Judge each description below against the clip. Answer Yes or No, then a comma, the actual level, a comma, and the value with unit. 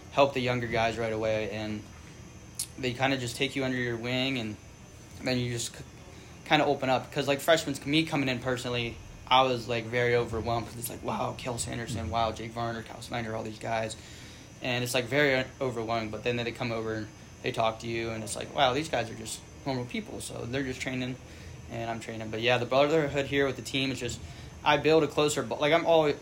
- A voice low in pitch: Yes, low, 120 Hz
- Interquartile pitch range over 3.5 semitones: No, average, 2.8 semitones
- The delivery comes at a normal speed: No, fast, 235 wpm